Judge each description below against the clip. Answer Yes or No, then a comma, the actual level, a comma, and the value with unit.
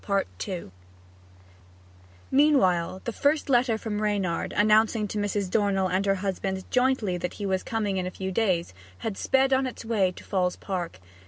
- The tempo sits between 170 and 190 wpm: No, average, 160 wpm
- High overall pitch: Yes, high, 205 Hz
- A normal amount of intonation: Yes, average, 3.3 semitones